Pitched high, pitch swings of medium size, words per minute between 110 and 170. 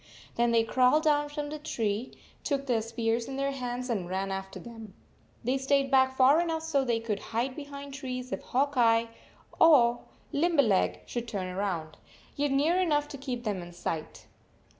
No: very high, 255 Hz; average, 3.8 semitones; average, 180 wpm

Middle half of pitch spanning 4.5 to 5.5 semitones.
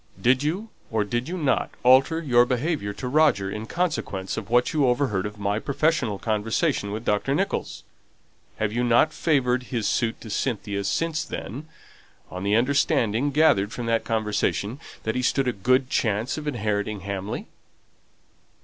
Yes: average, 5.1 semitones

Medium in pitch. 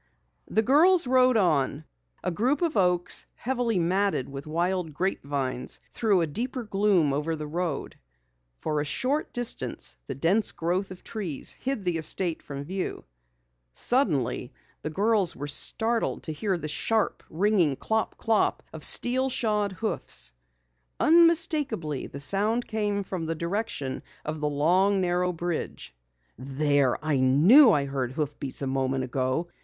Yes: medium, 180 Hz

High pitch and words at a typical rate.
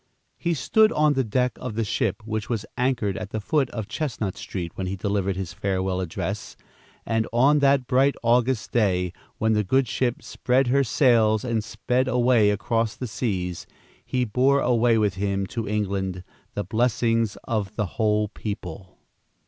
No: low, 110 Hz; average, 170 wpm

